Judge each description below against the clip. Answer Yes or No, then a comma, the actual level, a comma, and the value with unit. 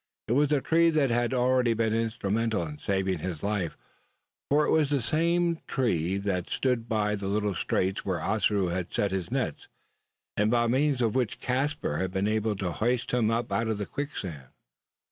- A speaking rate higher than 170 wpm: Yes, average, 185 wpm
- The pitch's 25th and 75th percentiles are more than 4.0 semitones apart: Yes, average, 5.0 semitones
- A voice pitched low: Yes, low, 110 Hz